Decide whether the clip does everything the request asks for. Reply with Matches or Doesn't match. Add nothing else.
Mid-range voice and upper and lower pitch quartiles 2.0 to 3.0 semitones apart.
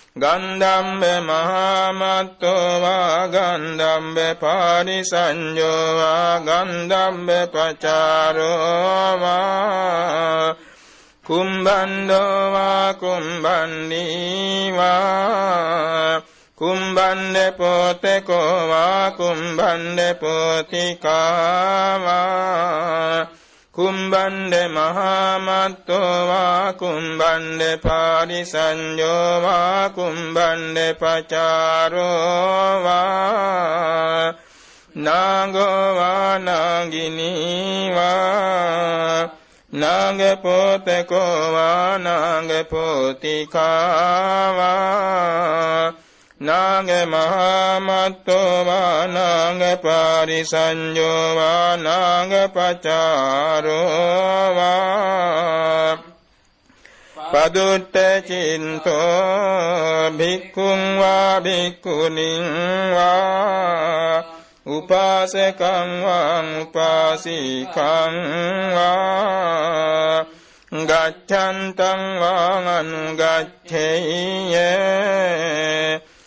Matches